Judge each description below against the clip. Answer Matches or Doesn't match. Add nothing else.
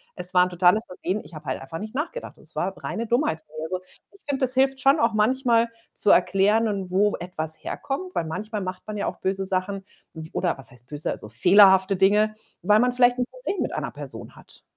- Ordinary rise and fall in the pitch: Matches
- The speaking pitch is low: Doesn't match